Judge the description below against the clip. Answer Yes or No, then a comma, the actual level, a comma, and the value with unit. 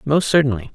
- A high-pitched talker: No, low, 135 Hz